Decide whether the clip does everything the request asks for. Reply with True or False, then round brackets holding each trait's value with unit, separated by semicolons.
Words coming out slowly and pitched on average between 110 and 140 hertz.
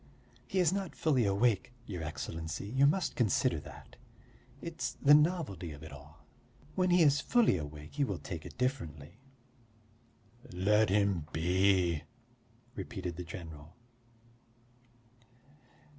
False (125 wpm; 100 Hz)